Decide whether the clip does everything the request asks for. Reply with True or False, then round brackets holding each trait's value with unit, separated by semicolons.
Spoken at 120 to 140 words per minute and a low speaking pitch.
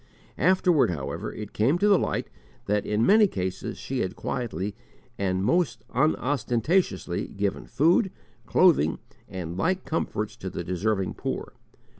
True (135 wpm; 110 Hz)